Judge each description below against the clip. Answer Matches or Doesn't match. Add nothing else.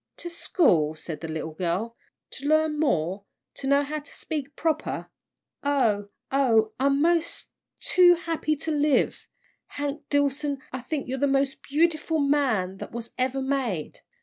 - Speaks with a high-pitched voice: Matches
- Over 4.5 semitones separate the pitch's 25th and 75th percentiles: Matches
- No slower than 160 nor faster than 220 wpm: Doesn't match